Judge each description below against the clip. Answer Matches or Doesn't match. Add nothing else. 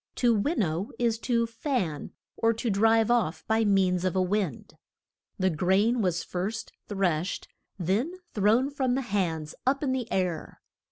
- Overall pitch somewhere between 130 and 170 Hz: Doesn't match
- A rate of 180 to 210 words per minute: Doesn't match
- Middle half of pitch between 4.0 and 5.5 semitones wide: Matches